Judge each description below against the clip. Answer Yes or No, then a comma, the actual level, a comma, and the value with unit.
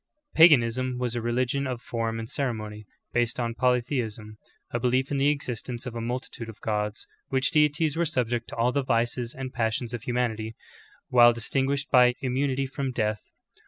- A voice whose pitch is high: No, low, 125 Hz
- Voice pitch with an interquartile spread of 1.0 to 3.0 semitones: Yes, narrow, 2.4 semitones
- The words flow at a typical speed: Yes, average, 185 wpm